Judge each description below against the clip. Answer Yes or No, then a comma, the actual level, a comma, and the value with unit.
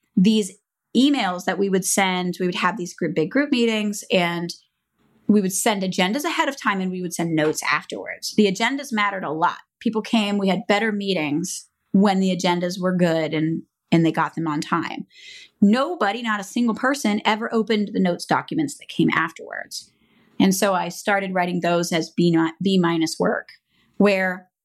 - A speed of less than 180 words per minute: No, average, 185 wpm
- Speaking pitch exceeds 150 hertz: Yes, high, 190 Hz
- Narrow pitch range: No, average, 3.6 semitones